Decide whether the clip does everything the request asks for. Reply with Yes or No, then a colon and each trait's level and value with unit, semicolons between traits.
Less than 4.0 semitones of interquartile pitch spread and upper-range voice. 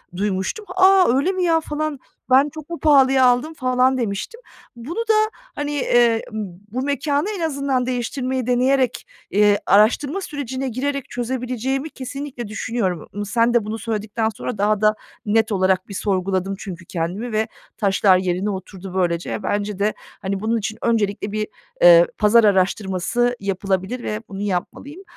No: average, 5.3 semitones; high, 235 Hz